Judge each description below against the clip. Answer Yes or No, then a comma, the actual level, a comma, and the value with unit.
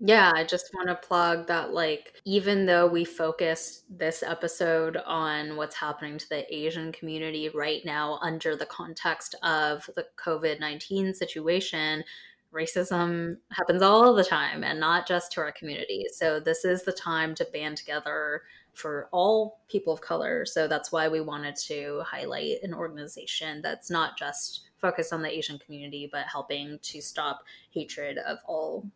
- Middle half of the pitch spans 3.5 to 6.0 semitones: No, average, 2.7 semitones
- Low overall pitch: No, medium, 165 Hz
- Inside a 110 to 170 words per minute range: Yes, average, 165 wpm